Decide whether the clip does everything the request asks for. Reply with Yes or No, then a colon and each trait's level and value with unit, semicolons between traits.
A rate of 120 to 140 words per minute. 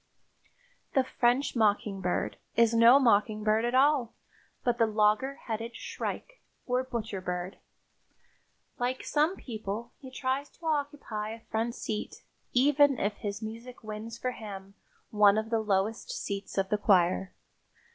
Yes: slow, 135 wpm